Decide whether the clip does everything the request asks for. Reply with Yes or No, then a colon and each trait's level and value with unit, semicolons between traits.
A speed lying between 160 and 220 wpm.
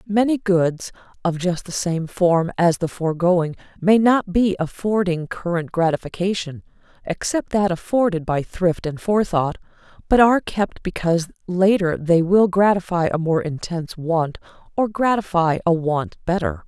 No: average, 145 wpm